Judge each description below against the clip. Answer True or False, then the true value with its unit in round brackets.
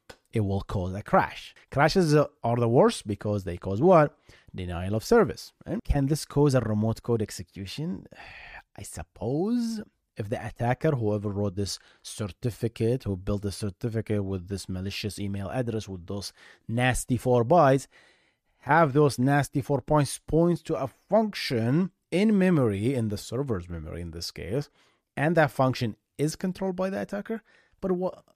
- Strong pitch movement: True (6.8 semitones)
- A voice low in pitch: True (120 Hz)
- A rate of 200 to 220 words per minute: False (160 wpm)